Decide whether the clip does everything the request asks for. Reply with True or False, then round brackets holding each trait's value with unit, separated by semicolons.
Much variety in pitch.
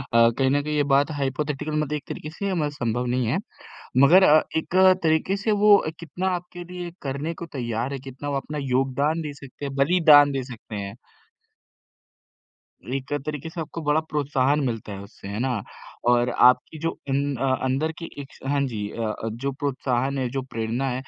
False (3.2 semitones)